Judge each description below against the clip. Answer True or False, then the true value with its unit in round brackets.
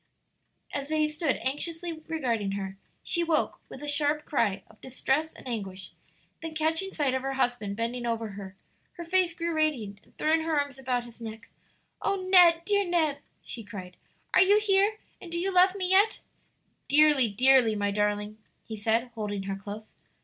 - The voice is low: False (270 Hz)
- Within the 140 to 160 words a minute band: False (180 wpm)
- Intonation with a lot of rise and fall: True (7.2 semitones)